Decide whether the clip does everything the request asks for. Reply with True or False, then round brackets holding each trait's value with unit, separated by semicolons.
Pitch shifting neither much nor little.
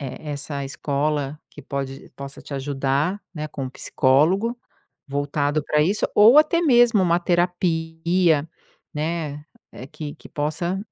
True (3.9 semitones)